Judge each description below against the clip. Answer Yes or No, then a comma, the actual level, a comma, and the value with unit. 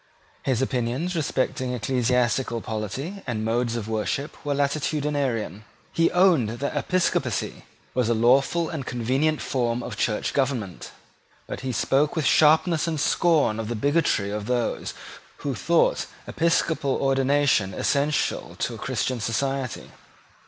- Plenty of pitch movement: No, average, 4.3 semitones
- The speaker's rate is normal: No, slow, 130 wpm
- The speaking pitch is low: Yes, low, 130 Hz